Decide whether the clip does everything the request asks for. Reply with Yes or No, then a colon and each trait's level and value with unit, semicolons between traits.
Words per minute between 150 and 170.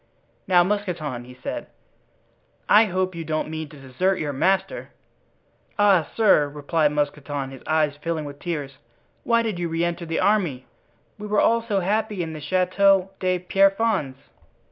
Yes: average, 160 wpm